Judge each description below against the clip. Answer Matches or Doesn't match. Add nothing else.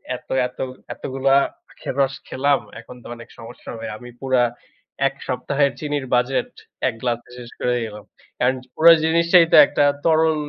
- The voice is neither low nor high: Doesn't match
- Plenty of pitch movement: Doesn't match